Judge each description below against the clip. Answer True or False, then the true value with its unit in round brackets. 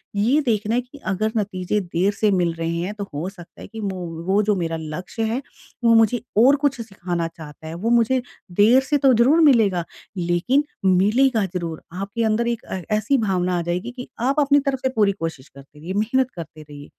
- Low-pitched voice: False (205 Hz)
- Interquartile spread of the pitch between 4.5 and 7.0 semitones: True (5.3 semitones)